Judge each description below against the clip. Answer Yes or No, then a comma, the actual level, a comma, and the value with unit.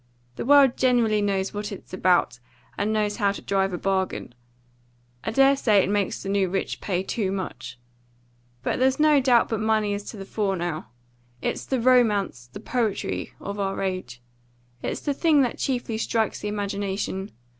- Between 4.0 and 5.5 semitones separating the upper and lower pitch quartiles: No, average, 3.5 semitones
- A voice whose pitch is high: Yes, high, 205 Hz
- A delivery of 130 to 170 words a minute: No, average, 180 wpm